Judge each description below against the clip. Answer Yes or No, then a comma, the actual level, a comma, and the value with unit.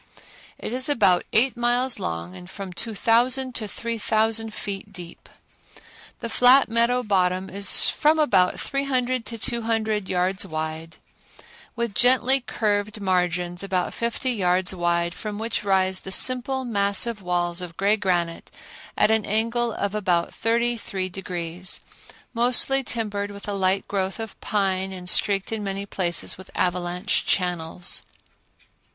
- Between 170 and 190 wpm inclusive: No, average, 145 wpm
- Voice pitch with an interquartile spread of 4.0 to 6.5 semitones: Yes, average, 4.3 semitones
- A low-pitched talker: No, high, 200 Hz